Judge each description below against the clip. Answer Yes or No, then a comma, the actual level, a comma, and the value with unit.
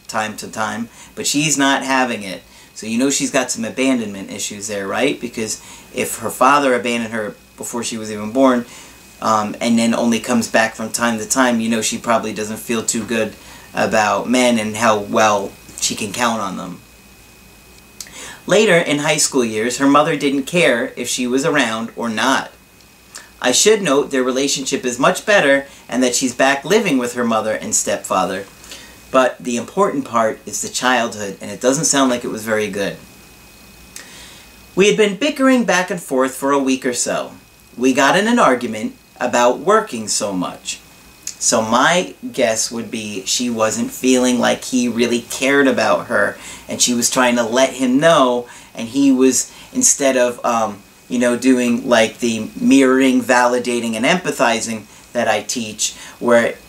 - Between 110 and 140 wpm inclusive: No, average, 180 wpm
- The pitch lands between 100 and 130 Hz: Yes, low, 125 Hz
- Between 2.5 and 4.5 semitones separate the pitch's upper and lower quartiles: Yes, average, 3.1 semitones